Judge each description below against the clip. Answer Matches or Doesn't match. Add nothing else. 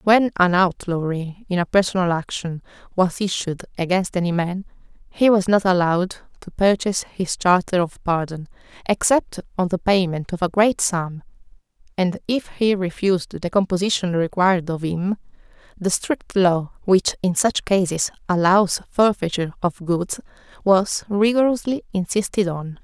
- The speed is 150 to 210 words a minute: Doesn't match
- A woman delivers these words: Matches